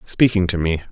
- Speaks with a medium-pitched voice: No, very low, 95 Hz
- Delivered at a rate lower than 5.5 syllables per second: No, 5.6 syllables/s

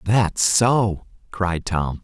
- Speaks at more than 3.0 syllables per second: No, 2.4 syllables/s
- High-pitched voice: No, very low, 95 Hz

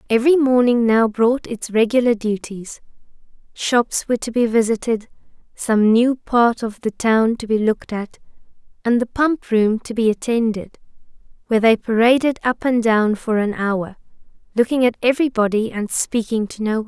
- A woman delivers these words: Yes, female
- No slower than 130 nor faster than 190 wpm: Yes, average, 160 wpm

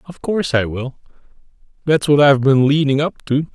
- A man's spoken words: Yes, male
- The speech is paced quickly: No, average, 185 wpm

